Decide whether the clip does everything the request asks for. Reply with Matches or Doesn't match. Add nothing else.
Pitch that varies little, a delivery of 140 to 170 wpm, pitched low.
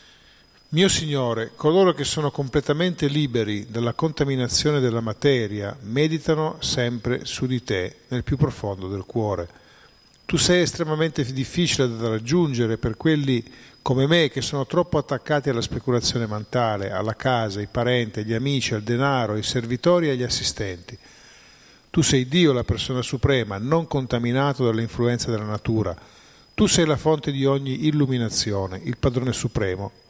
Doesn't match